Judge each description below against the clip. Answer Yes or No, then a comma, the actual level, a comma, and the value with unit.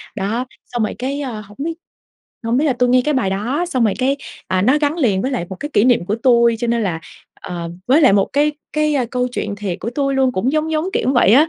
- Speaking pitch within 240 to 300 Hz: Yes, very high, 250 Hz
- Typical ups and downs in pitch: Yes, average, 4.8 semitones